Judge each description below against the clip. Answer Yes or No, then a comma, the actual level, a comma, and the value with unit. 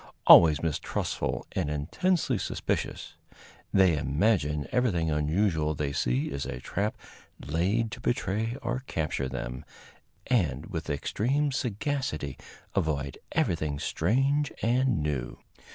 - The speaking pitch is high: No, very low, 80 Hz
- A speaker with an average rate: No, slow, 110 wpm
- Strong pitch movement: Yes, wide, 7.9 semitones